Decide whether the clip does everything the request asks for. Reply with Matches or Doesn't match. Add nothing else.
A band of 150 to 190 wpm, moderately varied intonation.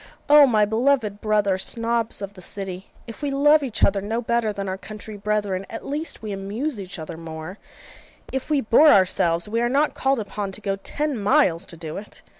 Doesn't match